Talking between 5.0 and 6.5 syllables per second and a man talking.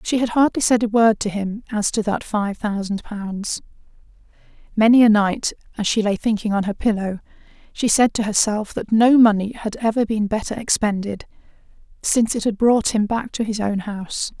No: 5.1 syllables/s; female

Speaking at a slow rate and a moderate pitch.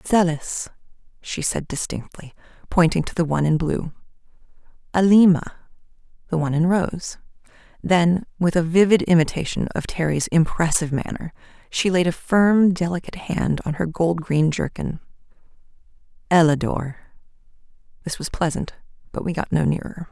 Yes: slow, 125 wpm; medium, 165 Hz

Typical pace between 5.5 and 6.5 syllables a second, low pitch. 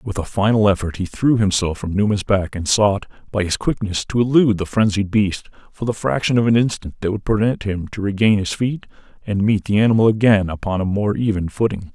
Yes: 5.6 syllables/s; low, 100 Hz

